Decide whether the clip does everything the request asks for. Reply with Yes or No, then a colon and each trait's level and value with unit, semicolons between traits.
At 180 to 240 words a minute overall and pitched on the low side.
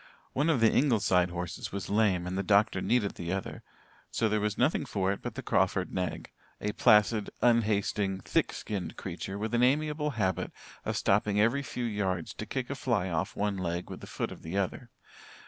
Yes: average, 200 wpm; low, 105 Hz